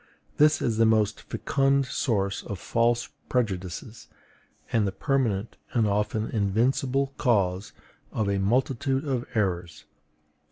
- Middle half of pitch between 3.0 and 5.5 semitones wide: Yes, average, 4.5 semitones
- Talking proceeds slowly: Yes, slow, 120 wpm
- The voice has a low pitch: Yes, low, 110 Hz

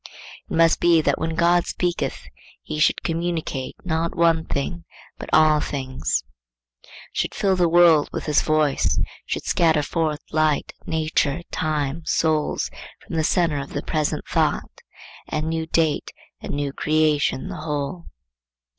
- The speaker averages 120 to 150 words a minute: Yes, average, 145 wpm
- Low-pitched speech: No, medium, 155 Hz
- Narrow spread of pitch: Yes, narrow, 1.9 semitones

